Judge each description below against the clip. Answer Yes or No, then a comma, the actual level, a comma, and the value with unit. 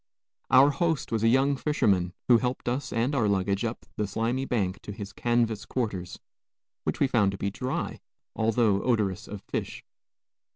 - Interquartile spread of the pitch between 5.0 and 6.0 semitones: No, average, 4.2 semitones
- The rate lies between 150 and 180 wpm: Yes, average, 170 wpm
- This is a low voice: Yes, low, 115 Hz